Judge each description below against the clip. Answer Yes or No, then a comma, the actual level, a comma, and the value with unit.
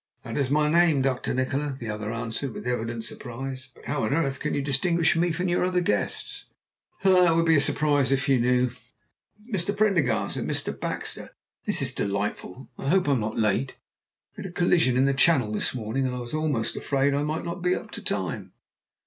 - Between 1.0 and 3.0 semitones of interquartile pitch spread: No, average, 5.1 semitones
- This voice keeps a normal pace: No, fast, 215 wpm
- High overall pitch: No, medium, 140 Hz